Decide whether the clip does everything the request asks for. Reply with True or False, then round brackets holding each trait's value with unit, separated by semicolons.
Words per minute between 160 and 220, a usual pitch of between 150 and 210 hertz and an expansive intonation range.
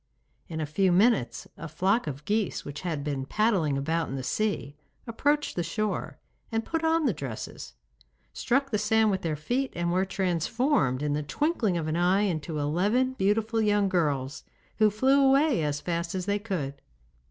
True (180 wpm; 190 Hz; 6.5 semitones)